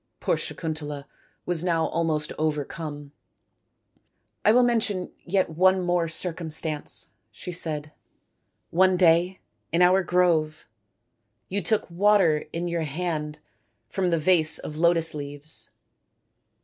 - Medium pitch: Yes, medium, 165 Hz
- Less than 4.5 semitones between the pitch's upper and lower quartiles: Yes, average, 2.8 semitones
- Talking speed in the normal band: No, slow, 125 wpm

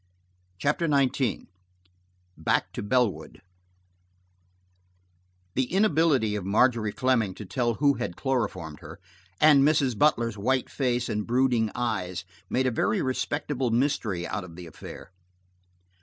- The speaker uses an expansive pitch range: No, average, 4.4 semitones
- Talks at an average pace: No, slow, 125 wpm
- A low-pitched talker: Yes, low, 120 Hz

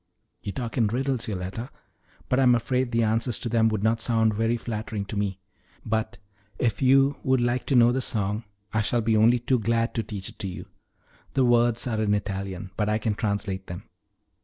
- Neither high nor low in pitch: No, low, 115 Hz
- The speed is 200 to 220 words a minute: Yes, fast, 205 wpm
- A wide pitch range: No, narrow, 2.6 semitones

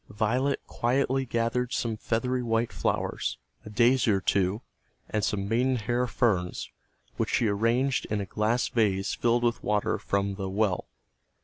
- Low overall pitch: Yes, low, 115 Hz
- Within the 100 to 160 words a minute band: Yes, average, 145 wpm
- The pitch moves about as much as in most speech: Yes, average, 3.1 semitones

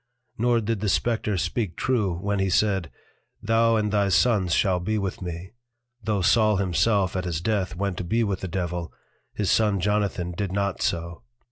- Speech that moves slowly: No, average, 180 wpm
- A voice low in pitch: Yes, low, 100 Hz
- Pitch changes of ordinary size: Yes, average, 3.0 semitones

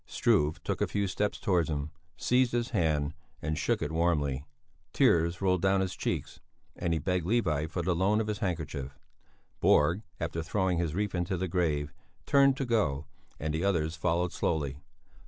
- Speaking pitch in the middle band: No, very low, 85 Hz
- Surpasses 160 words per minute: Yes, average, 175 wpm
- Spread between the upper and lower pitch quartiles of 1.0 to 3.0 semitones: No, average, 3.8 semitones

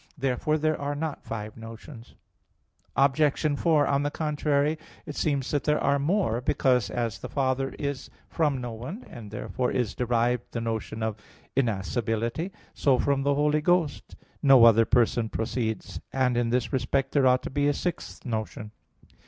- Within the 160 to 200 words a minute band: Yes, average, 165 wpm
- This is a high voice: No, low, 130 Hz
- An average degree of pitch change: Yes, average, 3.9 semitones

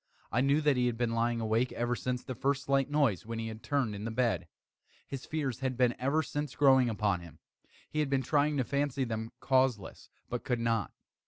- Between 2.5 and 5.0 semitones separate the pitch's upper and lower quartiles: Yes, average, 3.2 semitones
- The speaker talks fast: Yes, fast, 220 wpm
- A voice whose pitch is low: Yes, low, 125 Hz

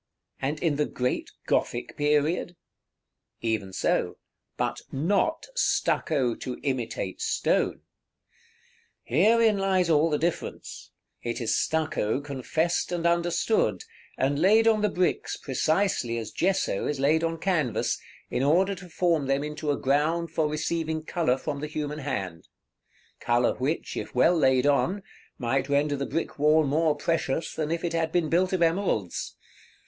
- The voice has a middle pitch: Yes, medium, 155 Hz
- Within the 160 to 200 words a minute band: No, average, 145 wpm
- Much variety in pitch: No, average, 4.0 semitones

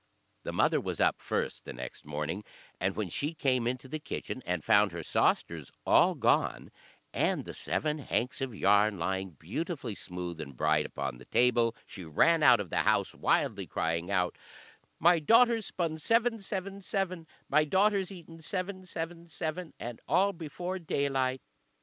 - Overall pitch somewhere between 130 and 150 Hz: Yes, low, 135 Hz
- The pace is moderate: Yes, average, 165 wpm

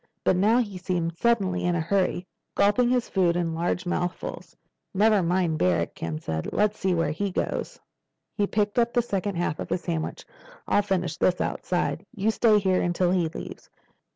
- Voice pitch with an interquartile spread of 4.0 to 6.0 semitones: No, average, 3.2 semitones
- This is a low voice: No, medium, 185 Hz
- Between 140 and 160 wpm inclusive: No, average, 180 wpm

